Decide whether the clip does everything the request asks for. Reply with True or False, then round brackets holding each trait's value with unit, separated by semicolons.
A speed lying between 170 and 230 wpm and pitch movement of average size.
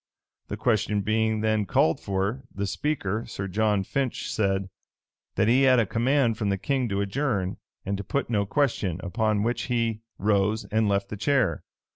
True (175 wpm; 3.3 semitones)